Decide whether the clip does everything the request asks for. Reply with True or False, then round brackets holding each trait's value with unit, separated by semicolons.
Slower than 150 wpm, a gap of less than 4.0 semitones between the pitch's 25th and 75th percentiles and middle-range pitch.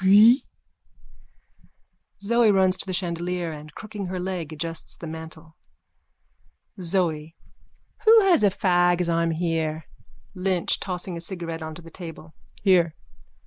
True (135 wpm; 2.7 semitones; 175 Hz)